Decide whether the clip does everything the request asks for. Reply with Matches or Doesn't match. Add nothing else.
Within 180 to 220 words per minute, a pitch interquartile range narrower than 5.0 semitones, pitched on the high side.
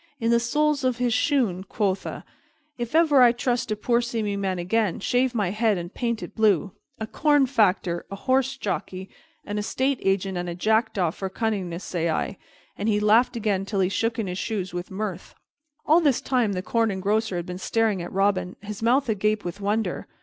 Matches